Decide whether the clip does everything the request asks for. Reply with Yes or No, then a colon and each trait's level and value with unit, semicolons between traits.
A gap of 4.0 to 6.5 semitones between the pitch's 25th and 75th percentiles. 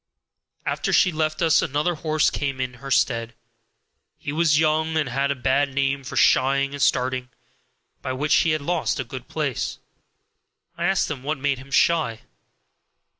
No: average, 3.0 semitones